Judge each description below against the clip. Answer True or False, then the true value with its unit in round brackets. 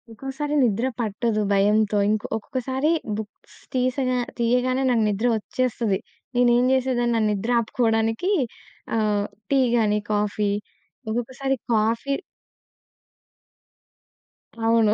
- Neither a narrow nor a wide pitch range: True (3.0 semitones)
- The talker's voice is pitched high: True (230 Hz)